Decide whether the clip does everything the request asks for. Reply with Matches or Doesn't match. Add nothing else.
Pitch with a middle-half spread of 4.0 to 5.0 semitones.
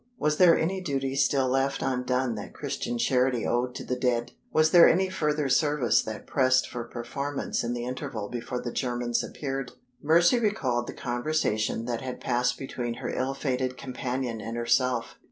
Doesn't match